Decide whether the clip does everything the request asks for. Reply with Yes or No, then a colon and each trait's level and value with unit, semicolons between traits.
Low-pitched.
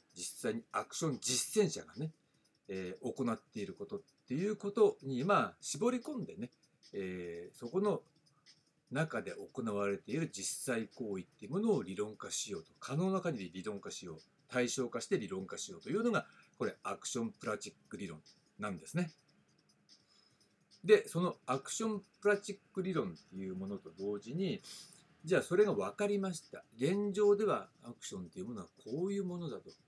No: medium, 170 Hz